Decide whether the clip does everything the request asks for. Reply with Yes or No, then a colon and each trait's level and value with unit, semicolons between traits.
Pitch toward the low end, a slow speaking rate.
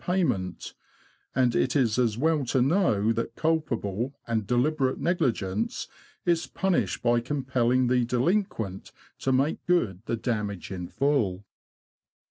Yes: low, 125 Hz; slow, 125 wpm